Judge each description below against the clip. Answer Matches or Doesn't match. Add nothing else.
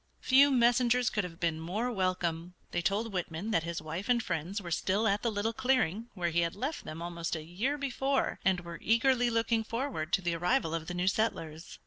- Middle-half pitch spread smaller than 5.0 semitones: Doesn't match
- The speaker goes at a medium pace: Doesn't match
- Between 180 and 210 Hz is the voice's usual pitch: Matches